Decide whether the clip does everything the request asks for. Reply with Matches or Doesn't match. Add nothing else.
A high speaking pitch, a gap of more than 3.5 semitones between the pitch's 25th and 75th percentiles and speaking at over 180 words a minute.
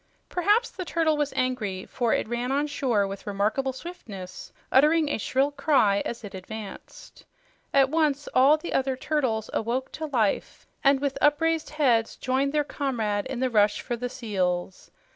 Doesn't match